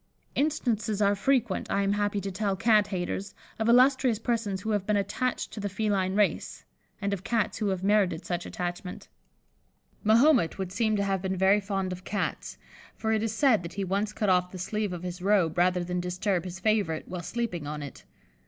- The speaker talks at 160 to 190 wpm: No, average, 200 wpm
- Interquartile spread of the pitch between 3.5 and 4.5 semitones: No, average, 2.9 semitones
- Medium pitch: No, high, 200 Hz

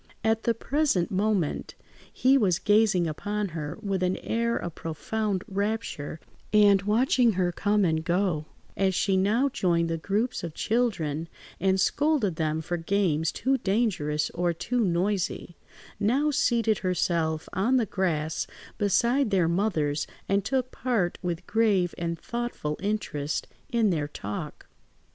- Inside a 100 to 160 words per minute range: Yes, average, 140 wpm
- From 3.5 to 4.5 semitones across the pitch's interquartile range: No, average, 4.9 semitones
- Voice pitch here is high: Yes, high, 195 Hz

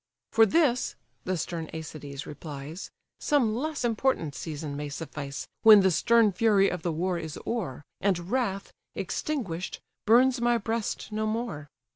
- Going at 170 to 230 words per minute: No, average, 145 wpm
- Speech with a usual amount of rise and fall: No, wide, 6.6 semitones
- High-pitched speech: Yes, high, 195 Hz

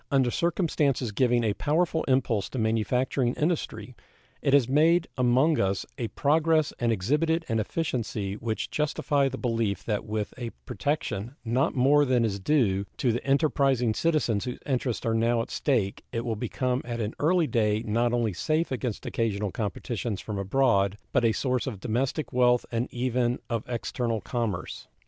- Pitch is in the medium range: No, low, 120 Hz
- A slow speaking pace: No, average, 165 wpm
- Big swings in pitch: No, average, 3.8 semitones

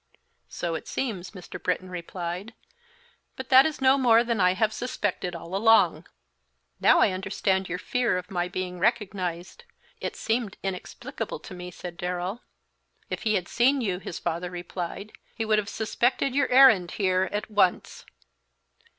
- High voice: Yes, high, 195 Hz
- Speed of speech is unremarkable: Yes, average, 160 wpm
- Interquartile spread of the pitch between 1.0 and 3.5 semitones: No, average, 4.2 semitones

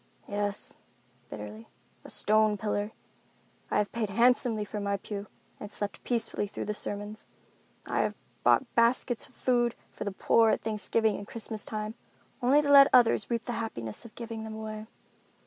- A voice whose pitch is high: Yes, high, 215 Hz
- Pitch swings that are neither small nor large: No, narrow, 2.2 semitones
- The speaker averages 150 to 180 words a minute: Yes, average, 165 wpm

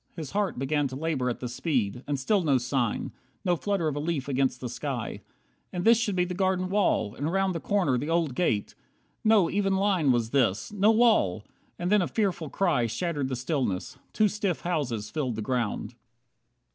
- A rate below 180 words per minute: No, average, 195 wpm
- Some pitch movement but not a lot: No, wide, 6.9 semitones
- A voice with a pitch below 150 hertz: No, medium, 155 Hz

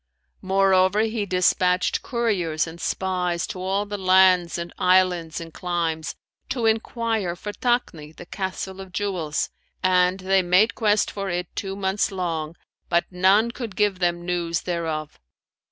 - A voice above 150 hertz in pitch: Yes, medium, 185 Hz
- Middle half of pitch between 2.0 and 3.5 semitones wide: Yes, narrow, 2.4 semitones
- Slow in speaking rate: No, average, 145 wpm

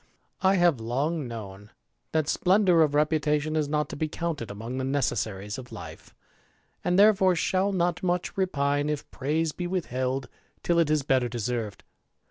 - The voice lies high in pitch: No, medium, 150 Hz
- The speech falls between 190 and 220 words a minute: No, average, 170 wpm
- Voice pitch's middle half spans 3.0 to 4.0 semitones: No, average, 5.3 semitones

